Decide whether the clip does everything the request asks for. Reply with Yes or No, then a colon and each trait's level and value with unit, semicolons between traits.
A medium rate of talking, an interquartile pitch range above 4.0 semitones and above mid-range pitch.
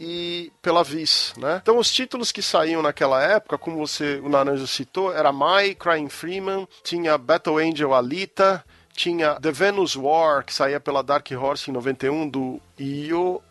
No: average, 165 wpm; average, 4.4 semitones; medium, 160 Hz